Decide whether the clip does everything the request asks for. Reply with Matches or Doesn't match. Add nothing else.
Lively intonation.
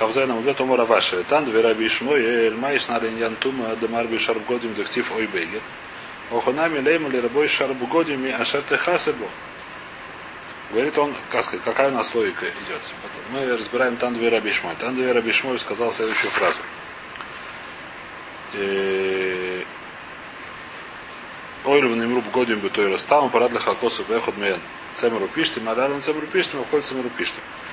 Doesn't match